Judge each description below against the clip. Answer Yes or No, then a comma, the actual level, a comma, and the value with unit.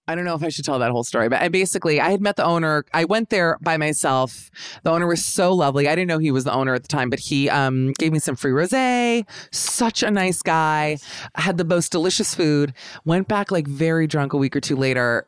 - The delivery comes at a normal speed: No, fast, 260 wpm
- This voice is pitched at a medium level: Yes, medium, 160 Hz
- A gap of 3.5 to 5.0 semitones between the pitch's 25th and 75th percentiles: Yes, average, 4.2 semitones